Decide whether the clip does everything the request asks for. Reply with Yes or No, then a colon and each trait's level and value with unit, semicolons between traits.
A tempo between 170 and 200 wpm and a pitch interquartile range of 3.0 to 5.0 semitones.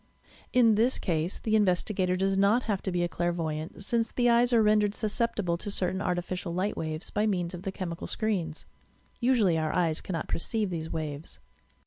Yes: average, 190 wpm; average, 4.0 semitones